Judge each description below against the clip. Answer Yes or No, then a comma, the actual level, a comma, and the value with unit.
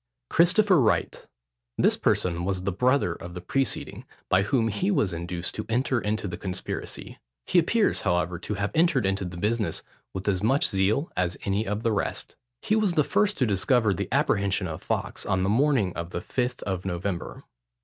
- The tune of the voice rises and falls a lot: Yes, wide, 6.0 semitones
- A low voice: Yes, low, 100 Hz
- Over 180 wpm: Yes, average, 190 wpm